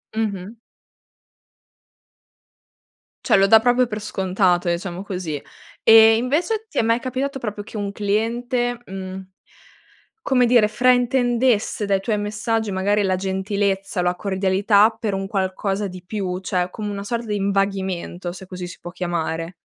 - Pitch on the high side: Yes, high, 200 Hz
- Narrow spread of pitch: No, average, 3.1 semitones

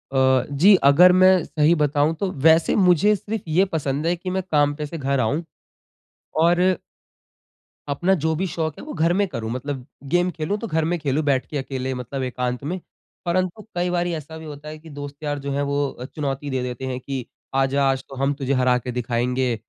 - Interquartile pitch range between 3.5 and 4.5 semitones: Yes, average, 4.2 semitones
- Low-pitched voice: No, medium, 145 Hz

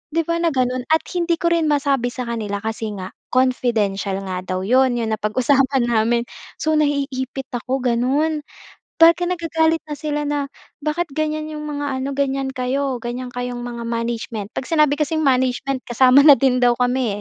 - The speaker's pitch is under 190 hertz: No, very high, 260 Hz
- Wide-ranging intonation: No, average, 3.9 semitones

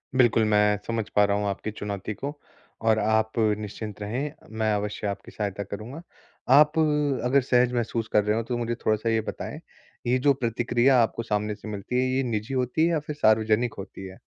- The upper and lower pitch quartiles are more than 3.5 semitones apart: No, average, 3.0 semitones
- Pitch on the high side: No, low, 110 Hz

